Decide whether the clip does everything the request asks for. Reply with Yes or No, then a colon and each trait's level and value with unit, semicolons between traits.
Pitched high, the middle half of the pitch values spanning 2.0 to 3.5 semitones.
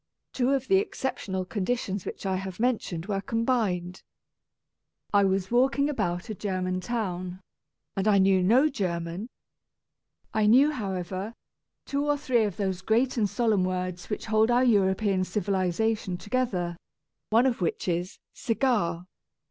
No: high, 200 Hz; average, 4.5 semitones